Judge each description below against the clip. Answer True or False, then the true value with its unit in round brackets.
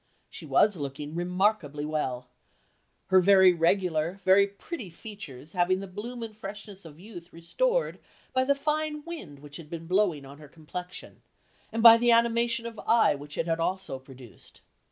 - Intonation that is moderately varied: False (6.3 semitones)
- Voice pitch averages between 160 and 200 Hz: True (185 Hz)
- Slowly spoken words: False (165 wpm)